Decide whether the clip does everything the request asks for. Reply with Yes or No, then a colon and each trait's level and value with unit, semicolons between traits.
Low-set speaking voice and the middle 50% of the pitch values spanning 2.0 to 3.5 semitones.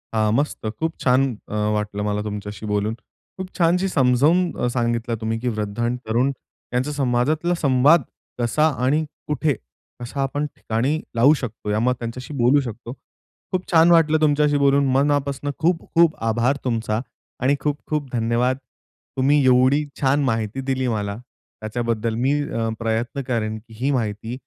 No: low, 125 Hz; average, 4.3 semitones